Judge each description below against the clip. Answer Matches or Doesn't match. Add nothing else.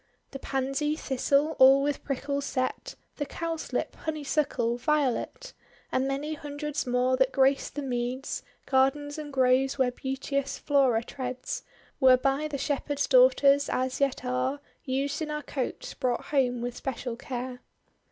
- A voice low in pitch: Doesn't match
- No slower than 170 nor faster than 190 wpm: Doesn't match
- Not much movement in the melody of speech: Matches